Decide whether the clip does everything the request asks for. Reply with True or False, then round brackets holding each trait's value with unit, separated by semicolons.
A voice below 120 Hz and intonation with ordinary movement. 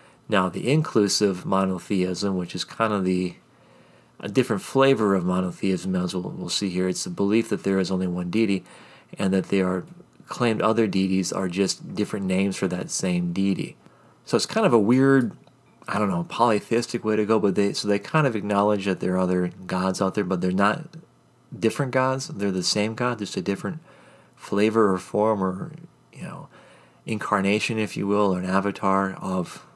True (100 Hz; 3.0 semitones)